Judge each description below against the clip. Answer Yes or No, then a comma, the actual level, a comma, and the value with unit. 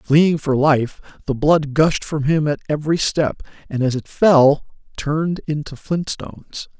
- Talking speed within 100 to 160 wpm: No, average, 170 wpm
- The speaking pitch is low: No, medium, 150 Hz